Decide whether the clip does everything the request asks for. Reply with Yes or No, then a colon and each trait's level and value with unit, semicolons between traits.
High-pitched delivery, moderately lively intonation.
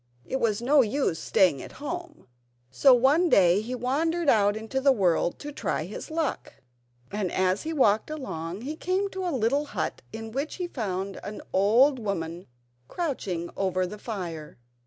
No: high, 230 Hz; wide, 7.4 semitones